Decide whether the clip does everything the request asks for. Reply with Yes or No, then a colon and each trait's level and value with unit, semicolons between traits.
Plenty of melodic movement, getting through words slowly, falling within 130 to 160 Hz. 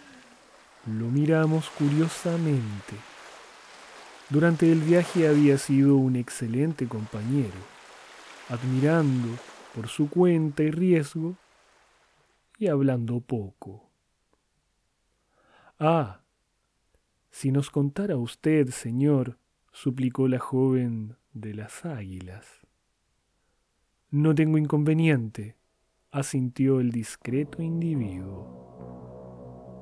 Yes: wide, 5.7 semitones; slow, 80 wpm; low, 135 Hz